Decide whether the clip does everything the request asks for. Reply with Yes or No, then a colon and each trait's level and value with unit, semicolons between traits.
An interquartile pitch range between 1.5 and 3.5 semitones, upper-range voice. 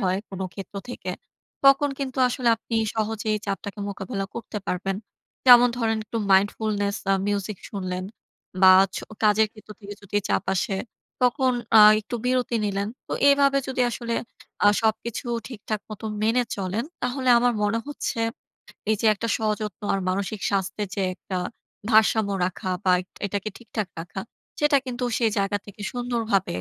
Yes: average, 3.1 semitones; high, 215 Hz